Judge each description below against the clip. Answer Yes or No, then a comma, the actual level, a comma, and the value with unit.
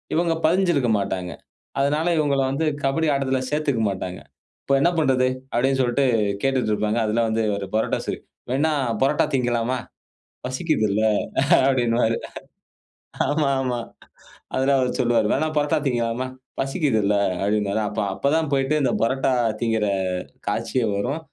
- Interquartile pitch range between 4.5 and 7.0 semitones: No, average, 3.8 semitones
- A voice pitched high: No, low, 130 Hz